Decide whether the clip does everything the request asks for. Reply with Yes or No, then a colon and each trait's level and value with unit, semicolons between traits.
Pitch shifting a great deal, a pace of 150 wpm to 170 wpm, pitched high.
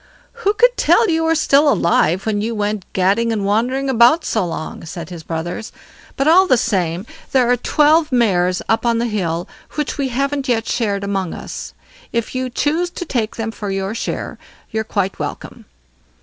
No: wide, 5.9 semitones; average, 185 wpm; high, 230 Hz